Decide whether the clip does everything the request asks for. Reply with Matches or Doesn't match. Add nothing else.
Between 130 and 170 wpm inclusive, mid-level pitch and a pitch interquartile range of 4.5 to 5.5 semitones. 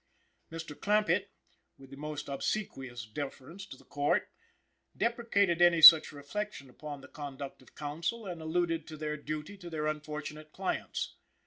Doesn't match